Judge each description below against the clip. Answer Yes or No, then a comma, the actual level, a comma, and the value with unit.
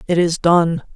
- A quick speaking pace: No, average, 190 wpm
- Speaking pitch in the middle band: Yes, medium, 170 Hz